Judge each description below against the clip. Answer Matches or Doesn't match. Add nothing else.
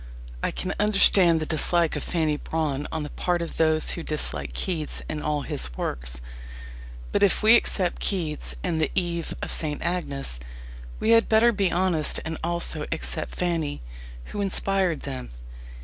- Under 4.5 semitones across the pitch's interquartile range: Matches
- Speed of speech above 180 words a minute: Doesn't match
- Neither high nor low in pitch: Matches